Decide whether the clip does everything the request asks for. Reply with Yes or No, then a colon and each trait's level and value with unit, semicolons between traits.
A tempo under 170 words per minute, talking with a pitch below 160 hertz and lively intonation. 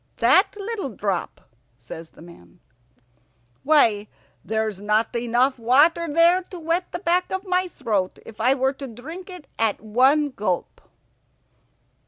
No: average, 140 wpm; very high, 260 Hz; wide, 7.9 semitones